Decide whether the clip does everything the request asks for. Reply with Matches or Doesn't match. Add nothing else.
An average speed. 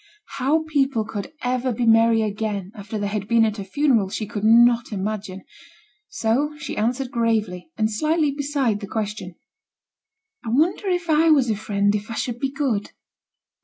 Matches